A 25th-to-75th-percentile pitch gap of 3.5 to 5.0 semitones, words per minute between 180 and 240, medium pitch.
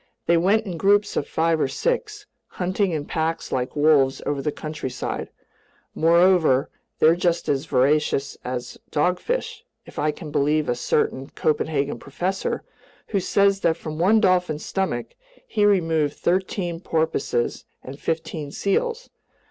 No: average, 4.3 semitones; average, 140 wpm; medium, 160 Hz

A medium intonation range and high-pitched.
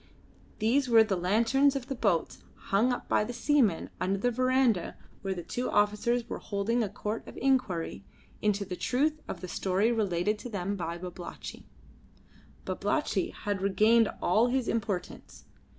Yes: average, 4.3 semitones; high, 215 Hz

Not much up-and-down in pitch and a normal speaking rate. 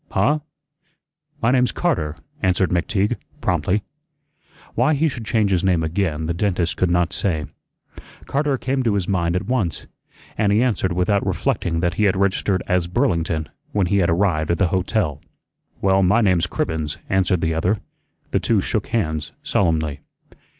No: average, 3.8 semitones; average, 165 wpm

